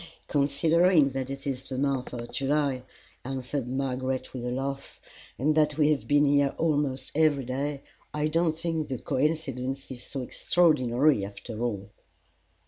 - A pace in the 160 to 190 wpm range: No, average, 150 wpm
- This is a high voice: No, medium, 140 Hz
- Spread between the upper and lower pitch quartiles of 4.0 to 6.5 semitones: No, average, 2.7 semitones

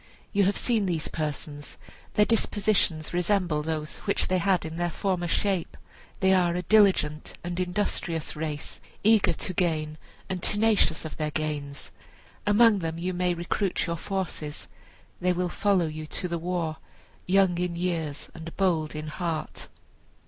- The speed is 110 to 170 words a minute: Yes, average, 155 wpm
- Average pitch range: Yes, average, 3.3 semitones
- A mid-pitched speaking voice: Yes, medium, 175 Hz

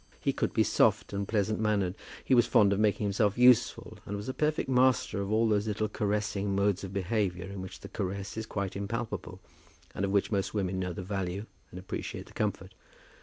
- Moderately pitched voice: No, low, 100 Hz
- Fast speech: Yes, fast, 210 wpm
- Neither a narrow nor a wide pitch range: No, narrow, 1.8 semitones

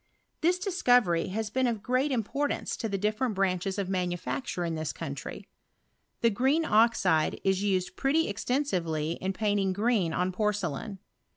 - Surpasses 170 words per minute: No, average, 160 wpm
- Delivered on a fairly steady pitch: No, average, 5.2 semitones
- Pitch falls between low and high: No, high, 205 Hz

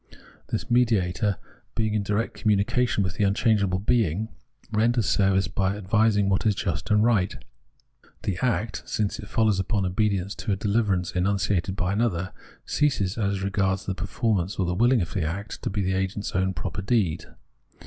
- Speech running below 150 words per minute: No, average, 175 wpm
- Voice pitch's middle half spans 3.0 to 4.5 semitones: No, narrow, 2.5 semitones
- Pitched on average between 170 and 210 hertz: No, low, 100 Hz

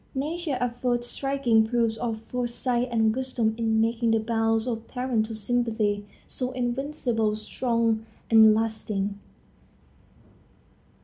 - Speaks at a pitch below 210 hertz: No, high, 230 Hz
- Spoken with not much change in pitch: Yes, narrow, 2.0 semitones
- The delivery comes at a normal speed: No, slow, 110 wpm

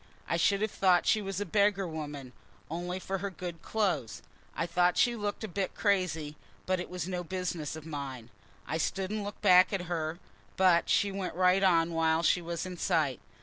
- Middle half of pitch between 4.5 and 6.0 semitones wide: No, average, 3.1 semitones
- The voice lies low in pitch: No, medium, 180 Hz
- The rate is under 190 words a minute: No, average, 200 wpm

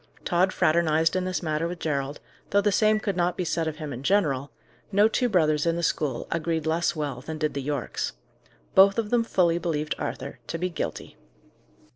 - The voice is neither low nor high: Yes, medium, 165 Hz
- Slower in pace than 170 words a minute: No, average, 200 wpm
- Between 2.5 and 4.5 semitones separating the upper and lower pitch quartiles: Yes, average, 3.4 semitones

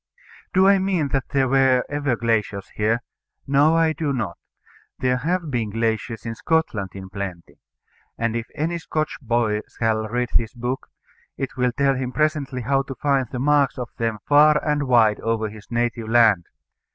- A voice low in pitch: Yes, low, 125 Hz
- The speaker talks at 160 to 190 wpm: Yes, average, 175 wpm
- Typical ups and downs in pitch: Yes, average, 4.3 semitones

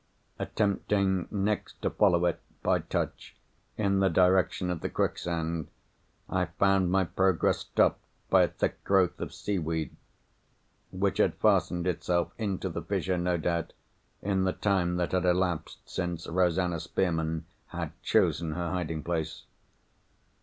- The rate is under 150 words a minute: Yes, slow, 135 wpm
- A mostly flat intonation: Yes, narrow, 2.1 semitones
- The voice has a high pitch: No, very low, 90 Hz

